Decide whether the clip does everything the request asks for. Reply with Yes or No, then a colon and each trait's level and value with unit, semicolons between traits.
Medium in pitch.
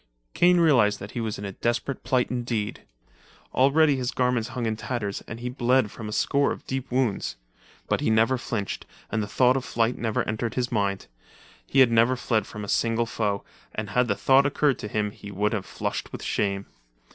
No: low, 115 Hz